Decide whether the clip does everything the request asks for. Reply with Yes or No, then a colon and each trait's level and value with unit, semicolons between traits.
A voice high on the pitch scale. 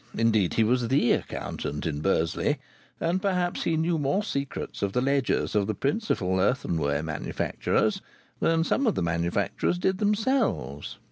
No: low, 125 Hz